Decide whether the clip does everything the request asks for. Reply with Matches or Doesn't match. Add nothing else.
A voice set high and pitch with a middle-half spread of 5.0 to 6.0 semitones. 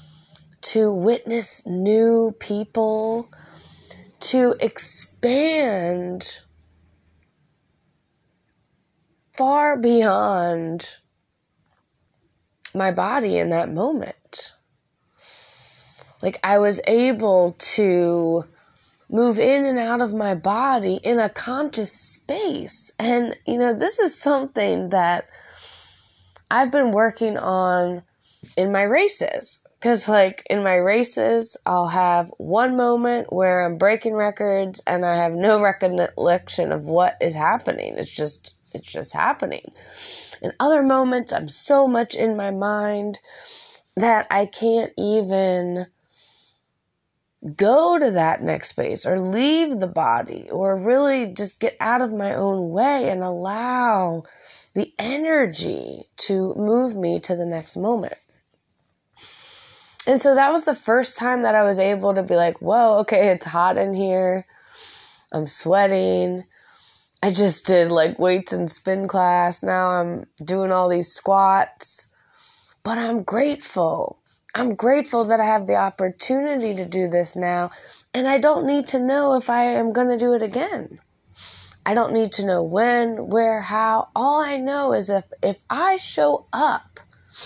Matches